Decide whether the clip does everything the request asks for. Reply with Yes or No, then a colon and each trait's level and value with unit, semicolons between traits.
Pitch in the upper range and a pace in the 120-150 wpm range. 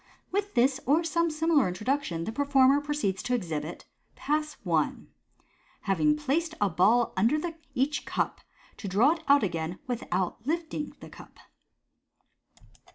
Yes: very high, 270 Hz; slow, 135 wpm